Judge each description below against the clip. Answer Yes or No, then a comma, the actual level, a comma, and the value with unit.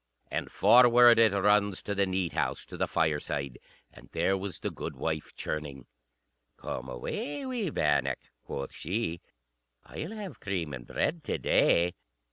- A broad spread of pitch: Yes, wide, 7.3 semitones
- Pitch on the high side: No, very low, 95 Hz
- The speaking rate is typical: Yes, average, 145 wpm